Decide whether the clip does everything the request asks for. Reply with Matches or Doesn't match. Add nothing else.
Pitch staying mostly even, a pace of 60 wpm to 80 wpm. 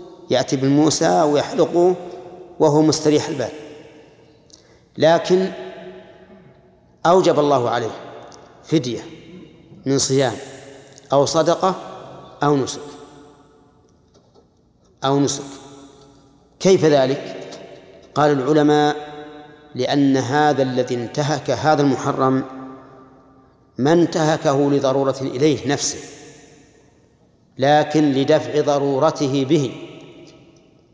Matches